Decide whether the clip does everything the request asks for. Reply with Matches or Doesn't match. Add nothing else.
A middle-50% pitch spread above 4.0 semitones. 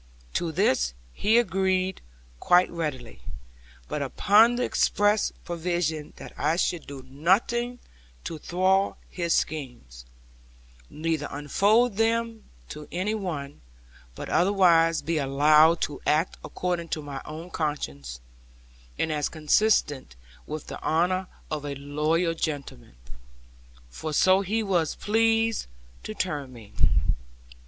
Matches